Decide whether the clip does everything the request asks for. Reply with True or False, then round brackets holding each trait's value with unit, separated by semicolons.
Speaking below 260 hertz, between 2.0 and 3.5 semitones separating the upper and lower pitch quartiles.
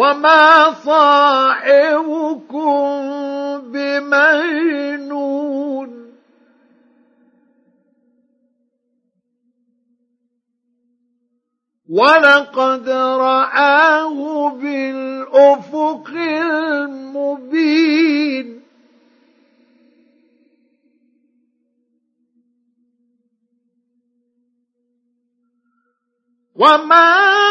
False (270 Hz; 2.7 semitones)